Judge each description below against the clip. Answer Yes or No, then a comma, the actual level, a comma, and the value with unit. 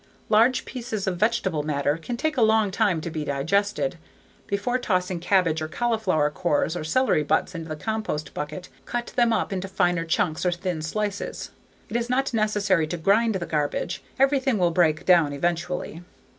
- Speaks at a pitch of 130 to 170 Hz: No, medium, 185 Hz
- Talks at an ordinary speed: Yes, average, 175 wpm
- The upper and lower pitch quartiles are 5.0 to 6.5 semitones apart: Yes, wide, 5.5 semitones